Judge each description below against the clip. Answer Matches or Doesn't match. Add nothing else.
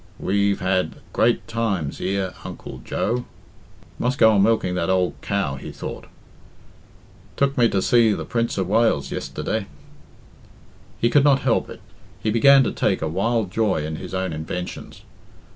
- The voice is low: Matches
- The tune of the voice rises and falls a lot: Doesn't match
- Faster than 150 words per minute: Matches